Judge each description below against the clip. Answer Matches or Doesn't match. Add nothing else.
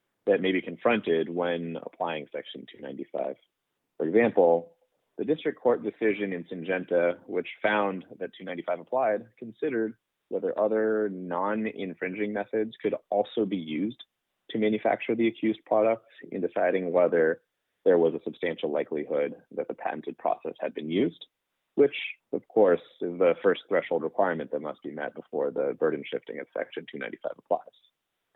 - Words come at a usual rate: Matches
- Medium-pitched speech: Doesn't match